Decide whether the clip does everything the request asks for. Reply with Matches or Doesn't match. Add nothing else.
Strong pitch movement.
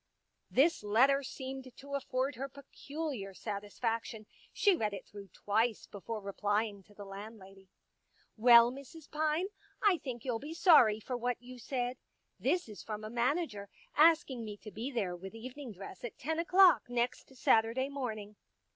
Doesn't match